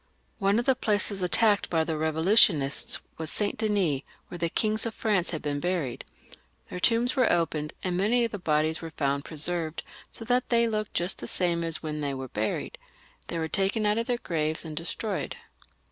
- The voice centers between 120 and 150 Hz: No, medium, 175 Hz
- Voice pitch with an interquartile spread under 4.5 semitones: No, average, 5.2 semitones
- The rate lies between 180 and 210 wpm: Yes, average, 195 wpm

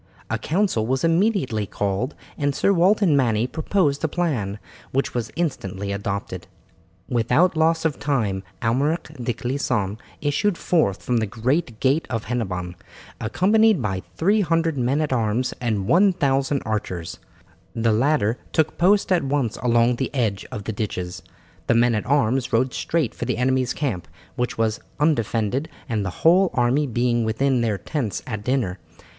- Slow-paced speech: No, average, 150 wpm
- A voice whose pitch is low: Yes, low, 125 Hz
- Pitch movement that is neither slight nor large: No, wide, 5.8 semitones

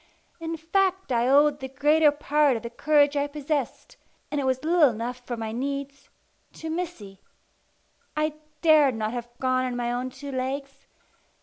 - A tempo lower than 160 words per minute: No, average, 170 wpm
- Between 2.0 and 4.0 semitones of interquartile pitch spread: Yes, average, 3.2 semitones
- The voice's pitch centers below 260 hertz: No, very high, 275 Hz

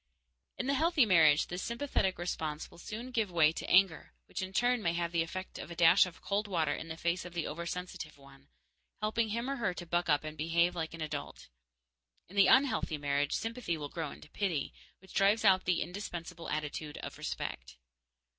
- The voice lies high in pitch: No, medium, 175 Hz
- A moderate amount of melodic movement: Yes, average, 4.2 semitones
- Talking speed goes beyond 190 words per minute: Yes, average, 200 wpm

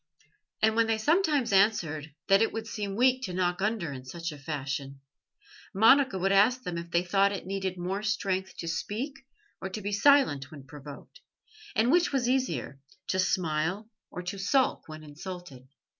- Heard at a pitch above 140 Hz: Yes, high, 190 Hz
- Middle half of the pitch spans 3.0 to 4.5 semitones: No, wide, 5.5 semitones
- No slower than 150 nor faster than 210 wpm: Yes, average, 175 wpm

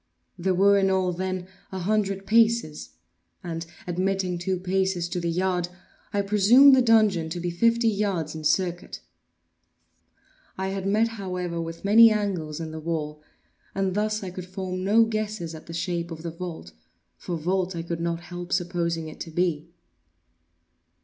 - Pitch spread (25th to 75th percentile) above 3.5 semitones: No, average, 2.8 semitones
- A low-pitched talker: No, medium, 185 Hz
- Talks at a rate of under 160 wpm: No, average, 165 wpm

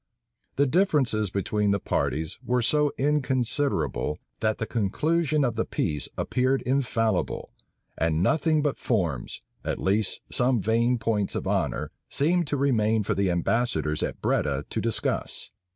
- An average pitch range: No, wide, 5.9 semitones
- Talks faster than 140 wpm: No, slow, 135 wpm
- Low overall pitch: Yes, low, 115 Hz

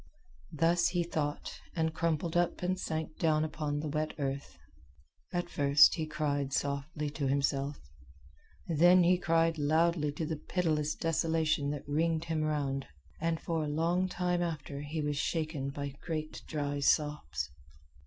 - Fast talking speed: No, average, 150 wpm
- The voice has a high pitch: No, medium, 155 Hz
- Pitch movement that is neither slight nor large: No, narrow, 2.3 semitones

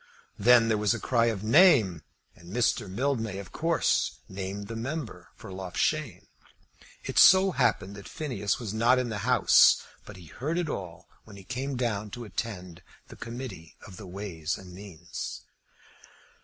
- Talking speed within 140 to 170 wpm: Yes, average, 160 wpm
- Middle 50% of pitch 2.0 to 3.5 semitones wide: No, average, 4.5 semitones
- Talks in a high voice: No, low, 105 Hz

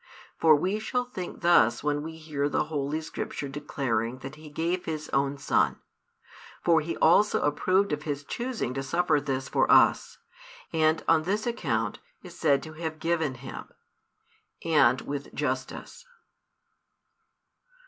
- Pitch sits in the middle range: Yes, medium, 155 Hz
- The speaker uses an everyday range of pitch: Yes, average, 3.3 semitones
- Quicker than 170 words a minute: No, average, 145 wpm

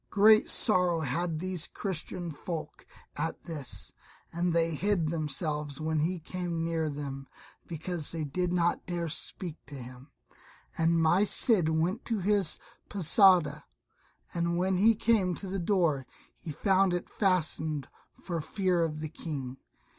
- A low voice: No, medium, 170 Hz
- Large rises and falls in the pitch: No, average, 3.1 semitones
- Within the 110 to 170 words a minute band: Yes, average, 145 wpm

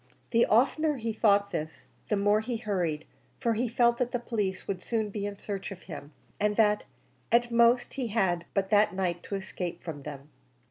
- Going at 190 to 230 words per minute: Yes, average, 200 wpm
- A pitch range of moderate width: Yes, average, 3.6 semitones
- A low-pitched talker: No, high, 210 Hz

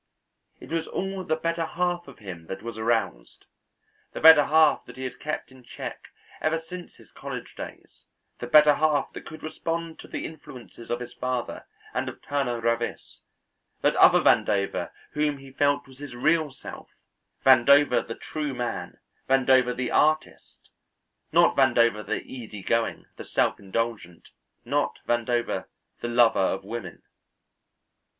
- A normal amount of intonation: Yes, average, 4.8 semitones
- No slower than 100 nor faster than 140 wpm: No, average, 155 wpm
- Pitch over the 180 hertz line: No, low, 130 Hz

